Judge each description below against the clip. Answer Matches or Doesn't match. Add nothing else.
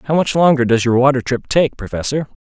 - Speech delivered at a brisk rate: Matches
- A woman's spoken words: Doesn't match